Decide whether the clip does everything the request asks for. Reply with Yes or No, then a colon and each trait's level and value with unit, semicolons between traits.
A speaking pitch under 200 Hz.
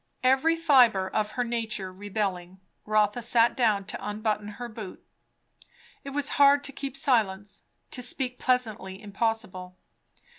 No: high, 220 Hz